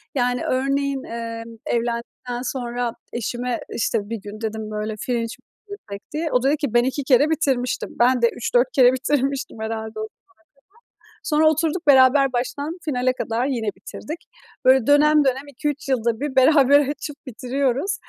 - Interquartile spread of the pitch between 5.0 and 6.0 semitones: No, average, 3.2 semitones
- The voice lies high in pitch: Yes, very high, 255 Hz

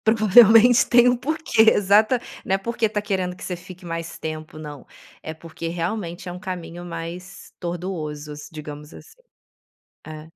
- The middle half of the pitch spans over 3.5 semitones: Yes, average, 4.6 semitones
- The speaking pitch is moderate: Yes, medium, 180 Hz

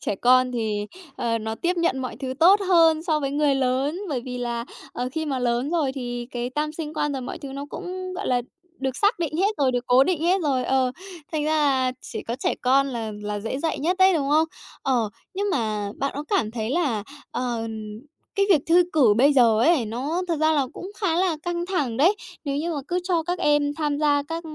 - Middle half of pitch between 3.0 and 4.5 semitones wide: No, average, 4.9 semitones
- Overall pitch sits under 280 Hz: No, very high, 285 Hz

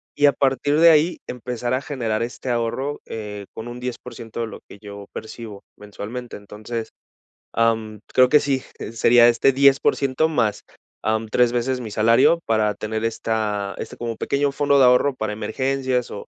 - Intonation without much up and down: No, average, 3.3 semitones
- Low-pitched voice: Yes, low, 120 Hz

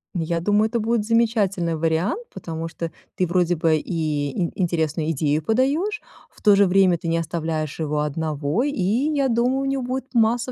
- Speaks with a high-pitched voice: No, medium, 180 Hz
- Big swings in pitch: Yes, wide, 6.4 semitones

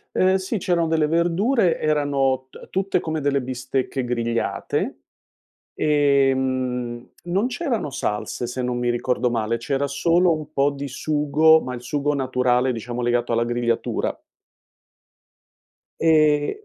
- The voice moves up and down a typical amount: Yes, average, 4.4 semitones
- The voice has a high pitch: No, medium, 140 Hz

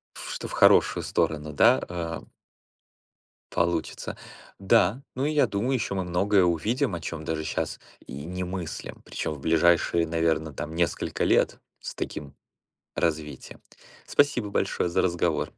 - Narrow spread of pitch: No, average, 3.6 semitones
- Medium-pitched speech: No, very low, 85 Hz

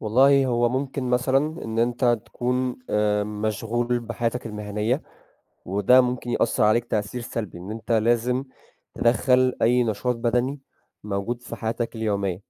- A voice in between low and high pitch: No, low, 120 Hz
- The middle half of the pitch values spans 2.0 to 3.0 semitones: Yes, average, 2.7 semitones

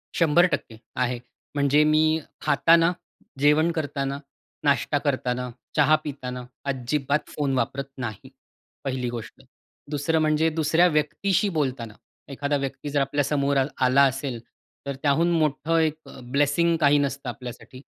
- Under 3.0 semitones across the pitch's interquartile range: Yes, narrow, 2.5 semitones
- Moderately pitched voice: Yes, medium, 145 Hz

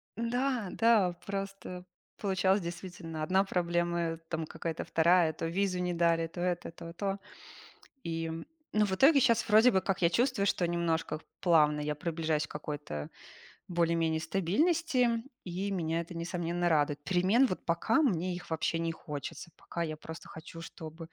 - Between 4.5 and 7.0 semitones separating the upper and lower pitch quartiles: No, average, 3.0 semitones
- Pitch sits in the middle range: Yes, medium, 175 Hz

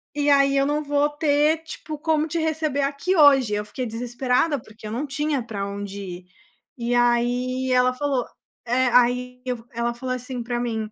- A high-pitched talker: Yes, very high, 255 Hz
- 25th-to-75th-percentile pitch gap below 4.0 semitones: Yes, average, 3.4 semitones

